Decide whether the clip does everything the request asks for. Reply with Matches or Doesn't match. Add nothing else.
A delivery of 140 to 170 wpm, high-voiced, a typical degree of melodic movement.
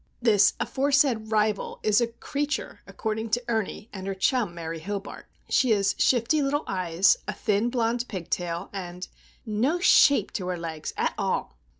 Matches